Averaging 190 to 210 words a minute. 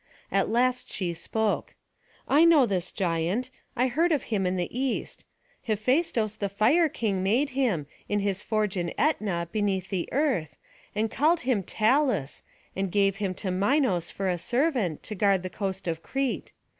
No: average, 170 wpm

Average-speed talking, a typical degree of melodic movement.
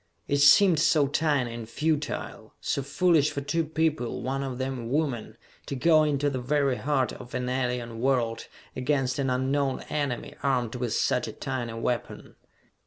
Yes: average, 170 wpm; average, 3.0 semitones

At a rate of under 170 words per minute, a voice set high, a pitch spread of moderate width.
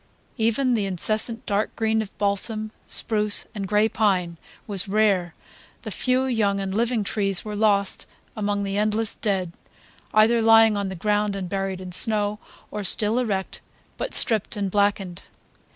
No: average, 155 wpm; high, 210 Hz; narrow, 2.0 semitones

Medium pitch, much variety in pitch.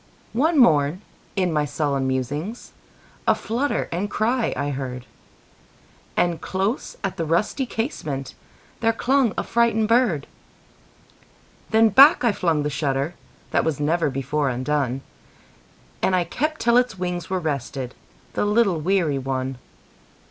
Yes: medium, 170 Hz; wide, 8.1 semitones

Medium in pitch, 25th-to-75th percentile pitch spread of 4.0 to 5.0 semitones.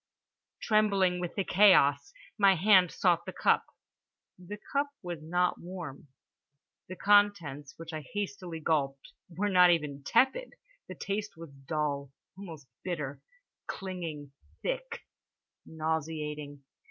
Yes: medium, 175 Hz; average, 4.7 semitones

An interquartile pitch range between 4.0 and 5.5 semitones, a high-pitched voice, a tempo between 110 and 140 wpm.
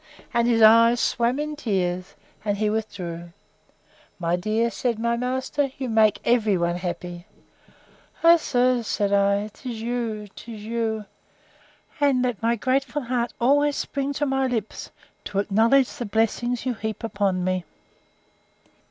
No: average, 3.6 semitones; high, 230 Hz; slow, 135 wpm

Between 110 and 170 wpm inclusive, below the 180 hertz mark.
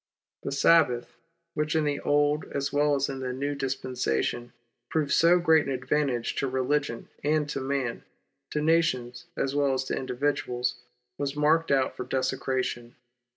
Yes: average, 165 wpm; medium, 140 Hz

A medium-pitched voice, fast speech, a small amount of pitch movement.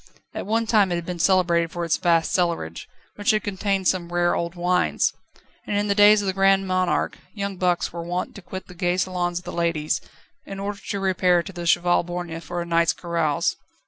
Yes: medium, 180 Hz; fast, 215 wpm; narrow, 2.2 semitones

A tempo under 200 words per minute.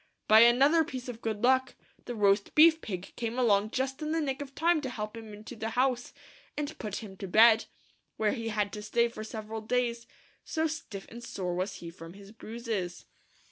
No: fast, 205 wpm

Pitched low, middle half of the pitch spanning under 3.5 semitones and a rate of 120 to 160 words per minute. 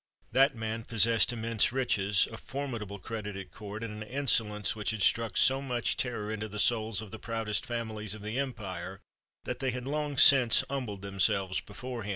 No: low, 110 Hz; average, 3.0 semitones; average, 190 wpm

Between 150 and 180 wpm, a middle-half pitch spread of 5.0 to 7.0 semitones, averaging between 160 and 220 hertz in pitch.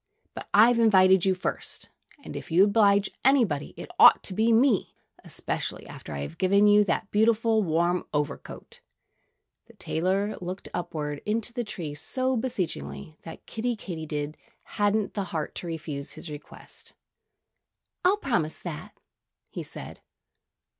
No: average, 140 wpm; wide, 5.6 semitones; high, 190 Hz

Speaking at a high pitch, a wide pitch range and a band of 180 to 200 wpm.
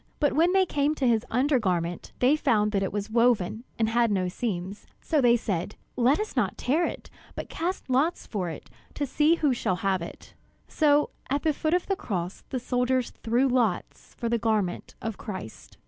Yes: high, 240 Hz; wide, 5.9 semitones; average, 195 wpm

